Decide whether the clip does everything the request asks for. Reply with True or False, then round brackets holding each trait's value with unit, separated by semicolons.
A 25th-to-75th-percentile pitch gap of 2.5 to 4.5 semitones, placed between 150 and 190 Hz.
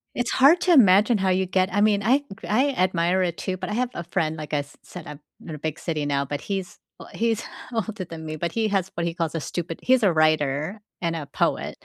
False (5.0 semitones; 185 Hz)